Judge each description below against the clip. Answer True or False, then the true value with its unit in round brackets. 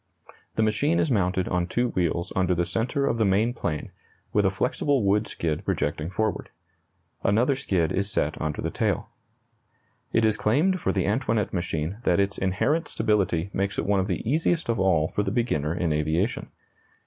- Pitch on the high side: False (100 Hz)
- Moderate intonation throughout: True (4.7 semitones)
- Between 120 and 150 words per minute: False (185 wpm)